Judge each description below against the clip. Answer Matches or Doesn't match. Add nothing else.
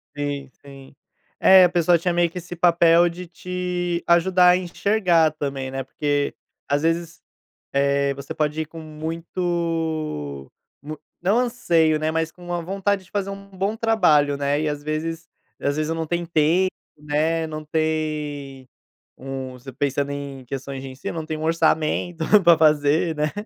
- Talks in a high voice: Doesn't match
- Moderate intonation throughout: Matches